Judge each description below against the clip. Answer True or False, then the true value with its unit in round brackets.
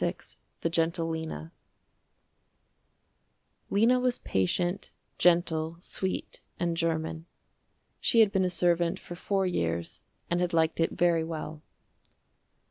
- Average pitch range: False (1.9 semitones)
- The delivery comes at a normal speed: False (120 wpm)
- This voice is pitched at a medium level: True (170 Hz)